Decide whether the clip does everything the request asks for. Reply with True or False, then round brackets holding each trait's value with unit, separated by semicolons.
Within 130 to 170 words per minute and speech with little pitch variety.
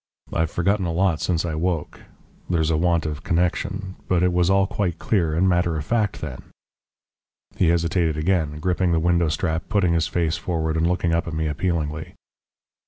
False (185 wpm; 2.2 semitones)